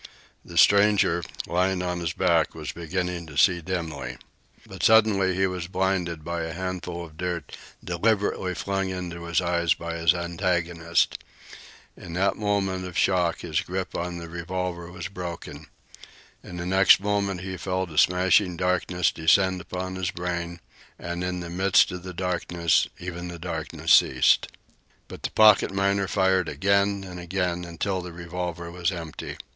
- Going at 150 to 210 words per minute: Yes, average, 160 wpm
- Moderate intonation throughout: No, narrow, 1.6 semitones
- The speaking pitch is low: Yes, very low, 90 Hz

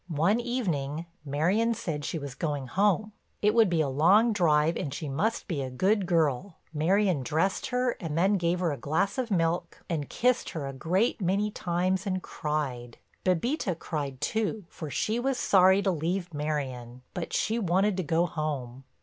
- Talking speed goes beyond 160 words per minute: Yes, average, 180 wpm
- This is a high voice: No, medium, 170 Hz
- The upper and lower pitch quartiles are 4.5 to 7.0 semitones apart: Yes, average, 5.2 semitones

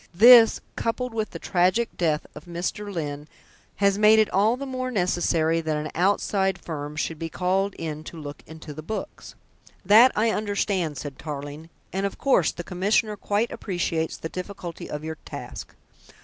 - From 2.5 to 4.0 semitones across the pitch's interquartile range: No, average, 4.7 semitones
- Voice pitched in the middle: Yes, medium, 180 Hz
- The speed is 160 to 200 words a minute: Yes, average, 170 wpm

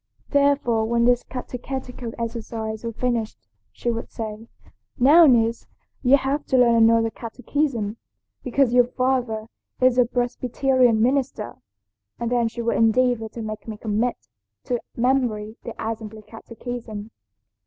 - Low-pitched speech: No, high, 235 Hz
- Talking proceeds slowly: Yes, slow, 130 wpm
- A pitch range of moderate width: No, narrow, 2.1 semitones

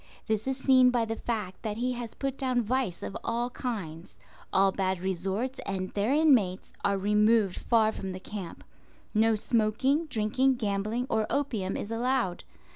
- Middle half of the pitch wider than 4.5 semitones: No, average, 4.1 semitones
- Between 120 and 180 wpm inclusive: Yes, average, 165 wpm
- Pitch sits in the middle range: No, high, 220 Hz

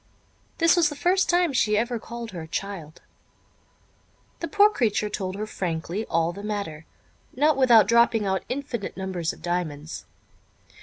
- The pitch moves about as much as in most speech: No, wide, 6.5 semitones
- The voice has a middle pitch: No, high, 210 Hz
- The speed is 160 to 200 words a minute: No, average, 150 wpm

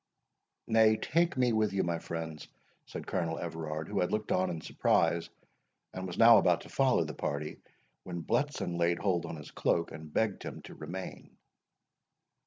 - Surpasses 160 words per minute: Yes, average, 175 wpm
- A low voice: Yes, very low, 85 Hz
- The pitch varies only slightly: No, average, 4.6 semitones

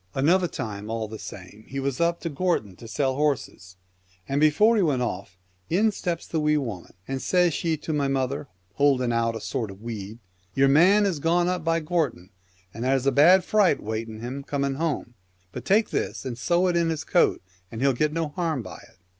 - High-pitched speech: No, medium, 140 Hz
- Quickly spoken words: Yes, fast, 215 wpm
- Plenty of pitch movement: Yes, wide, 6.2 semitones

